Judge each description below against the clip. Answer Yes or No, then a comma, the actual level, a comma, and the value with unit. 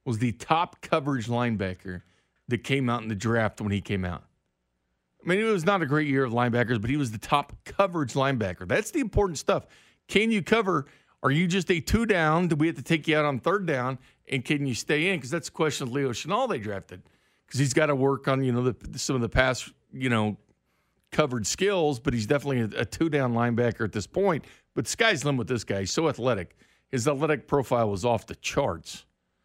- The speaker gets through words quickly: Yes, fast, 230 wpm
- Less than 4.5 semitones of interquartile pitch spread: No, average, 5.2 semitones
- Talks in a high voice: No, low, 130 Hz